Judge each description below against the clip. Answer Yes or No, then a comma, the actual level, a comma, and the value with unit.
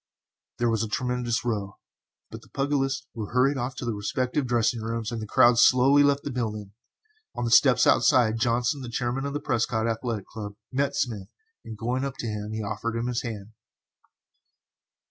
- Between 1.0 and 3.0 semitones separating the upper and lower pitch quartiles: Yes, narrow, 2.6 semitones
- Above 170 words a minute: Yes, average, 185 wpm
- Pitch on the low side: Yes, low, 120 Hz